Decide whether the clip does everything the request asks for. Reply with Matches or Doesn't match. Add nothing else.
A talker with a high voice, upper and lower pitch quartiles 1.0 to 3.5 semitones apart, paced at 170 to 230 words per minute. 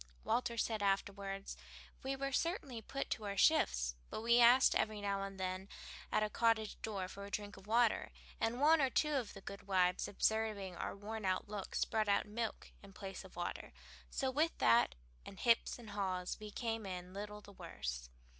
Matches